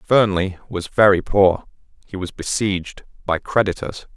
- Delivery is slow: Yes, slow, 130 wpm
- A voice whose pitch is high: No, very low, 95 Hz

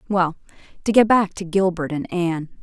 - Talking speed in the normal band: Yes, average, 185 wpm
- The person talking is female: Yes, female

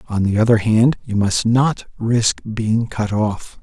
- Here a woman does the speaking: No, male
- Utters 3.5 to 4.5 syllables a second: Yes, 3.7 syllables/s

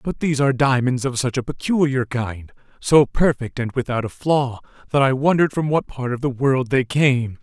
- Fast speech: Yes, fast, 210 wpm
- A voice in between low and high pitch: No, low, 130 Hz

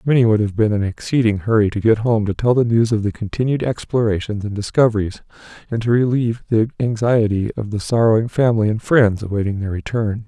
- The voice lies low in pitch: Yes, low, 110 Hz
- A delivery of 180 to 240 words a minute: Yes, average, 200 wpm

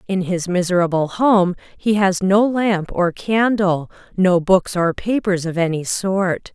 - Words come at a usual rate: Yes, average, 155 wpm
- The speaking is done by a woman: Yes, female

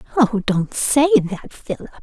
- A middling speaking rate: Yes, average, 150 wpm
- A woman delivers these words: Yes, female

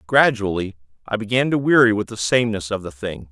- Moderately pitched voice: No, low, 105 Hz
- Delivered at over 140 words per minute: Yes, average, 200 wpm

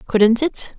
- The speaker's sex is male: No, female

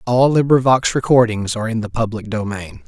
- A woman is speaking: No, male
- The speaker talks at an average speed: Yes, average, 165 wpm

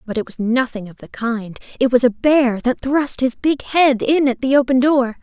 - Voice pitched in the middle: No, very high, 250 Hz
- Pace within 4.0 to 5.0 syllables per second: Yes, 4.7 syllables/s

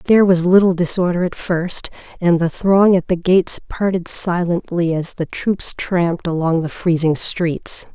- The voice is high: No, medium, 175 Hz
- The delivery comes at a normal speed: Yes, average, 165 wpm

